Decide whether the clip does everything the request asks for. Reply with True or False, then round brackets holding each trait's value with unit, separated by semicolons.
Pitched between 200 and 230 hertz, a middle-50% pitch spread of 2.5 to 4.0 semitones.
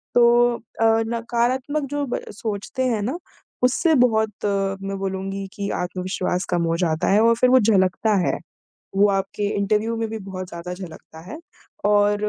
True (205 Hz; 3.2 semitones)